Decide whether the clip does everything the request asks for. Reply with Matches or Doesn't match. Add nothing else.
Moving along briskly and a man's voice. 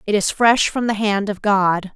Doesn't match